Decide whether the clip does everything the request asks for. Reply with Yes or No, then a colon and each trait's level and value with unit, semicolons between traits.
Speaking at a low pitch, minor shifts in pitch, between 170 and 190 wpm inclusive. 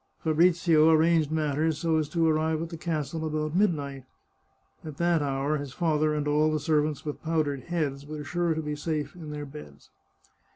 No: medium, 155 Hz; narrow, 1.6 semitones; average, 180 wpm